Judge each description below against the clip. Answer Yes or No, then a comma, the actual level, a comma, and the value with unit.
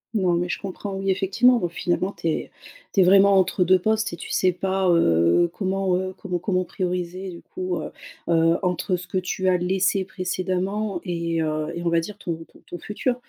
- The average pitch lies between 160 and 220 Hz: Yes, medium, 185 Hz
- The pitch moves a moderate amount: No, narrow, 1.9 semitones